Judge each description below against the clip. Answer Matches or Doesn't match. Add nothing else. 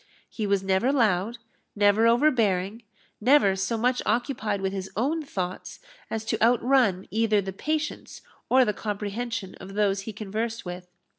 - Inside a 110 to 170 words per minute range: Matches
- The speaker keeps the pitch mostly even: Doesn't match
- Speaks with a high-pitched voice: Matches